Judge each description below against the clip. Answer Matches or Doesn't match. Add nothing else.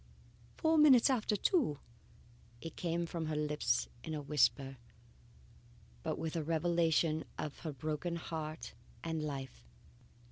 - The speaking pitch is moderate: Matches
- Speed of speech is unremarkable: Doesn't match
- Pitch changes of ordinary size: Doesn't match